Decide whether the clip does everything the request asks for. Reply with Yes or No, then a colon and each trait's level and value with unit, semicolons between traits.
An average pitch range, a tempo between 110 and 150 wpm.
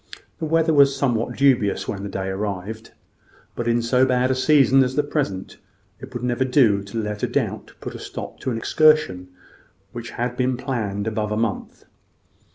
No: average, 4.1 semitones; average, 185 wpm